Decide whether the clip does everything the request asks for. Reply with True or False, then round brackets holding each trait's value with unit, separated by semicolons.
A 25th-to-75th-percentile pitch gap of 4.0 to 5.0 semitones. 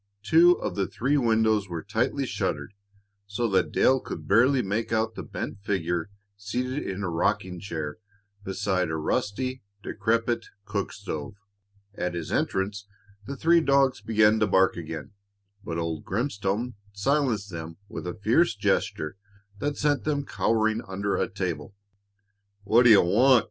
True (4.6 semitones)